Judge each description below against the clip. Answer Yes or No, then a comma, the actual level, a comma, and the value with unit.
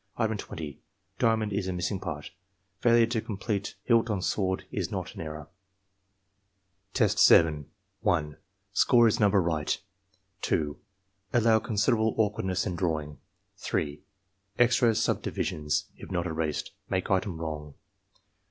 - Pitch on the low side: Yes, very low, 95 Hz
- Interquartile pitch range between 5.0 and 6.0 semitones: Yes, wide, 5.6 semitones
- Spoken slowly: Yes, slow, 125 wpm